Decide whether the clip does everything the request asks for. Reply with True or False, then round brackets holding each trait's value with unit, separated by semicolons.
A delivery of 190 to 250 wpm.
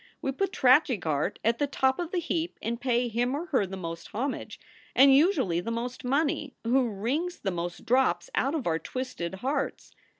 True (195 wpm)